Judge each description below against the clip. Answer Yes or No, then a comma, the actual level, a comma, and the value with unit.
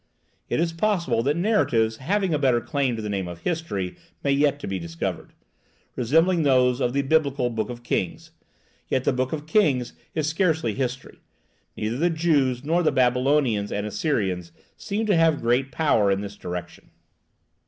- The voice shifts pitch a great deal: Yes, wide, 5.9 semitones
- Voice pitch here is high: No, low, 130 Hz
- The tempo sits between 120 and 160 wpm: No, average, 175 wpm